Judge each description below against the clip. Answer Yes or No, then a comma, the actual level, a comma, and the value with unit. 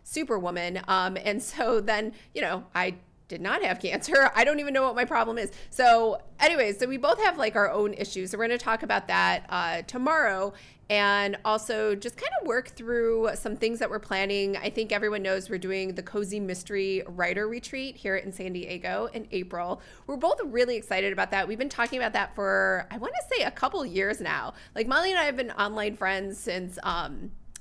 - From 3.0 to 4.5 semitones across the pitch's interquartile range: Yes, average, 3.6 semitones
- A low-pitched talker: No, high, 210 Hz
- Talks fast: Yes, fast, 215 wpm